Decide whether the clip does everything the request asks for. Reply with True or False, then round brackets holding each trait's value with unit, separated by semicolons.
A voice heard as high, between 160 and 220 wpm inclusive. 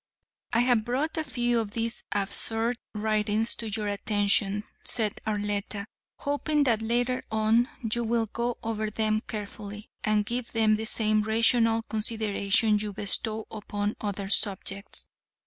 False (220 Hz; 140 wpm)